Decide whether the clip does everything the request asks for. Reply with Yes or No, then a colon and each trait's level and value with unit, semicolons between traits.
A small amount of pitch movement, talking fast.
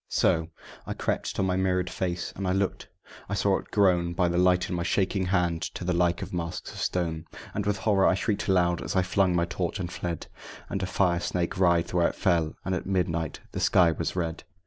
Yes: narrow, 1.7 semitones; fast, 235 wpm